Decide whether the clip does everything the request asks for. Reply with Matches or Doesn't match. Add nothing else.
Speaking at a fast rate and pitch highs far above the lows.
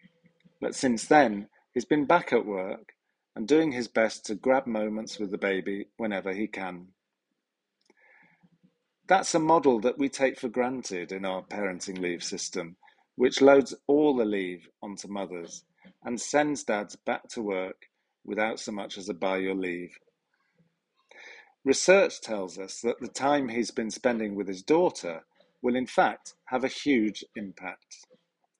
Doesn't match